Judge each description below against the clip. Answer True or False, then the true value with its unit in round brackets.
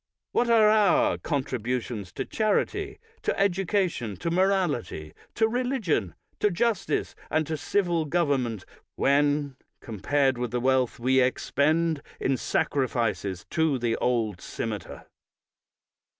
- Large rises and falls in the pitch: True (7.7 semitones)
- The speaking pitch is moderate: True (145 Hz)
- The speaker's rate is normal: False (115 wpm)